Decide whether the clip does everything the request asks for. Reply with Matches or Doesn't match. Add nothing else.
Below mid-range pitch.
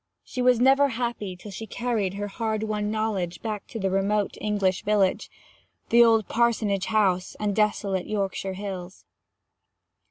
Doesn't match